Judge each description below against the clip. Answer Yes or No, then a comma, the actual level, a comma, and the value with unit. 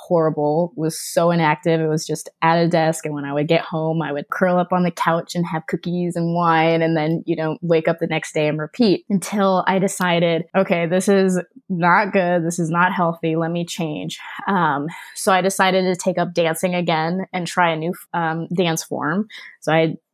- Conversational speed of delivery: No, fast, 215 wpm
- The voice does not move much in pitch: Yes, narrow, 2.2 semitones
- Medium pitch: Yes, medium, 170 Hz